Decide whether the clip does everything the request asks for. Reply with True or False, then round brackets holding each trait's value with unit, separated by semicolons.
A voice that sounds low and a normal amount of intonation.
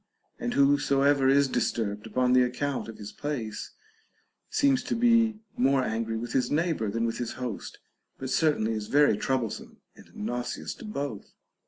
True (130 Hz; 4.1 semitones)